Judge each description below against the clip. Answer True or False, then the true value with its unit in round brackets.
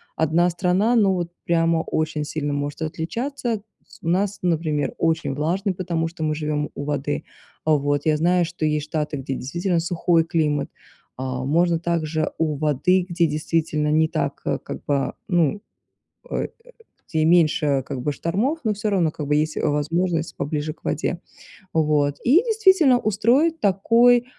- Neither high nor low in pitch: True (165 Hz)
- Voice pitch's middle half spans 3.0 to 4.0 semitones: True (3.5 semitones)